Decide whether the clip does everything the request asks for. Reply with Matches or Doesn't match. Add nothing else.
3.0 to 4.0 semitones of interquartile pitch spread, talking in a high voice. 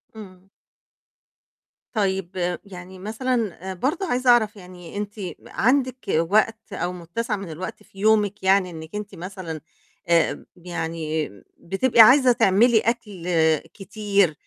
Matches